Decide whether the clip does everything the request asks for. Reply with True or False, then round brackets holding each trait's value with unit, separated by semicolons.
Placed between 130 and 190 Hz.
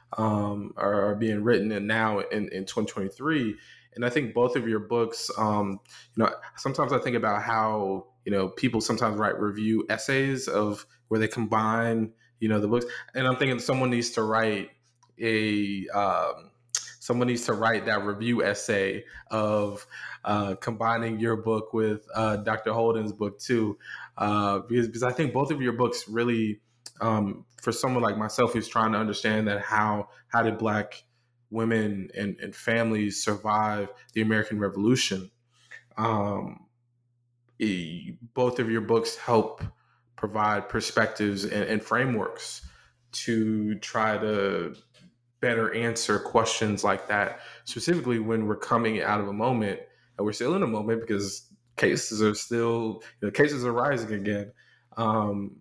False (110 Hz)